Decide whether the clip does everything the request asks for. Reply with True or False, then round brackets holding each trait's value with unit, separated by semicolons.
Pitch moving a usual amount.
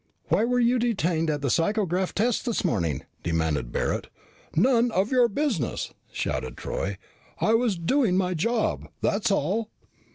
False (7.4 semitones)